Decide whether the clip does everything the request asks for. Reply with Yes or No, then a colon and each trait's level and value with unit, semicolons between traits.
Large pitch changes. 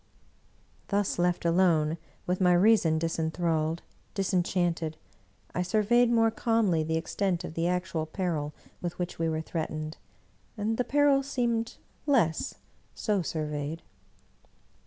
No: average, 4.4 semitones